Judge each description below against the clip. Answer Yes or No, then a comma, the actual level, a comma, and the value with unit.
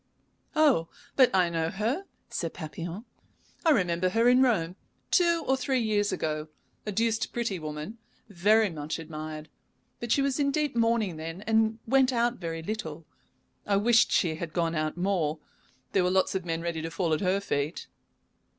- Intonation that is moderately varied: No, wide, 6.1 semitones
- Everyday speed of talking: Yes, average, 175 wpm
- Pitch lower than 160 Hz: No, high, 190 Hz